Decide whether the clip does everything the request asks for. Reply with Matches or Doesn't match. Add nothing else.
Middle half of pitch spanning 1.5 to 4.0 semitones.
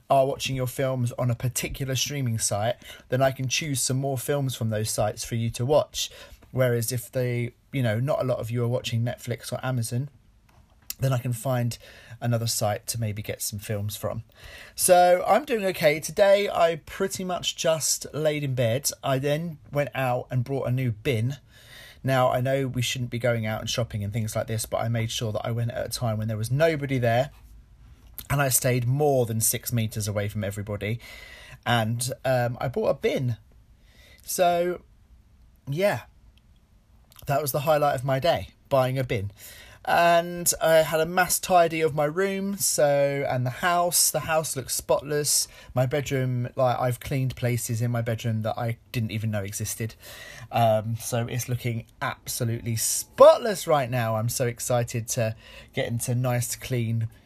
Matches